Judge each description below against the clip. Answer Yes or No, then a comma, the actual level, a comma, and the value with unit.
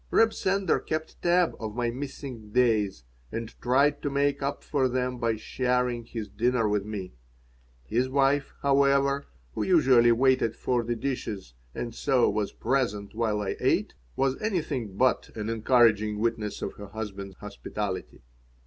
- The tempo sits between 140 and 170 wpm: Yes, average, 150 wpm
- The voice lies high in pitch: No, low, 120 Hz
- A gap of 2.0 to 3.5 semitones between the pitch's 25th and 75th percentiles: No, average, 4.2 semitones